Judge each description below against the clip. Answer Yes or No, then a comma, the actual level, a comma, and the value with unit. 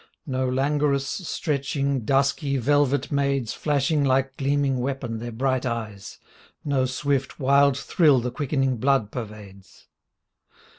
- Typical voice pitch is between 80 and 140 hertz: Yes, low, 135 Hz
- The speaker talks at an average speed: No, slow, 115 wpm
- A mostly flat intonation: Yes, narrow, 1.9 semitones